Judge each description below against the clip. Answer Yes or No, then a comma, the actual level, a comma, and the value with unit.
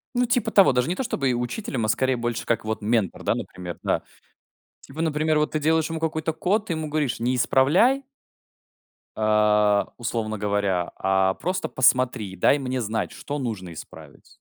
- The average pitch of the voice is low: Yes, low, 125 Hz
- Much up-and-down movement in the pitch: Yes, wide, 6.6 semitones